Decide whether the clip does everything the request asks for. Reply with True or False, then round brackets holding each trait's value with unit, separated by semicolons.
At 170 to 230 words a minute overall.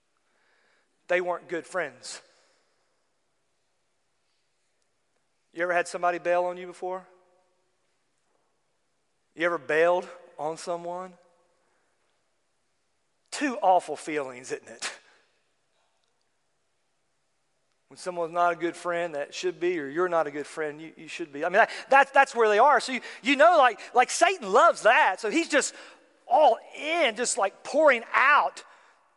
False (140 wpm)